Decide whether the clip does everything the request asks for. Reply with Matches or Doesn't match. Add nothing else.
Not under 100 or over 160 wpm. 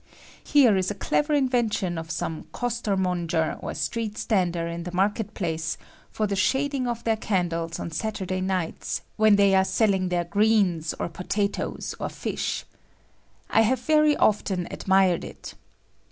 Matches